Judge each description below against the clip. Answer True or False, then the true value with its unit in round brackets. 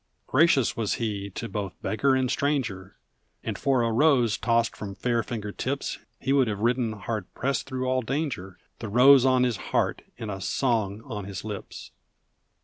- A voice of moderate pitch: False (115 Hz)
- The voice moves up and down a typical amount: True (4.0 semitones)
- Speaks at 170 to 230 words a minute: True (175 wpm)